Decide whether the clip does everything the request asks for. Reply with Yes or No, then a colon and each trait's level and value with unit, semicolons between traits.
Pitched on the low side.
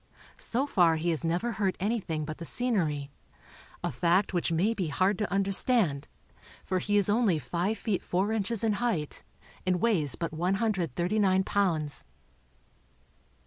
No: medium, 185 Hz